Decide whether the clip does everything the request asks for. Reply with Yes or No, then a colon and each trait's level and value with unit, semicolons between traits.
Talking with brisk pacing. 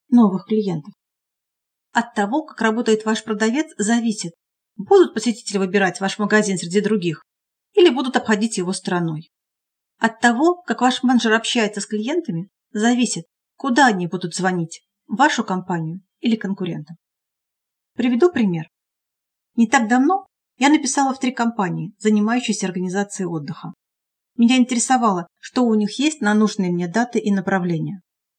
No: average, 135 wpm